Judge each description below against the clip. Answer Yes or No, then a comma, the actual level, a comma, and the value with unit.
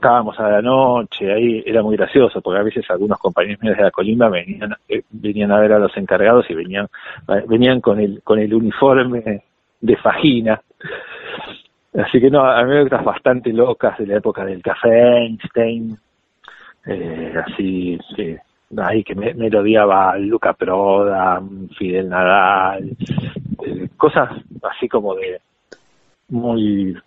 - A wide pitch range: No, average, 3.2 semitones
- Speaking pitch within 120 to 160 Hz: No, low, 110 Hz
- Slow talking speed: No, average, 145 wpm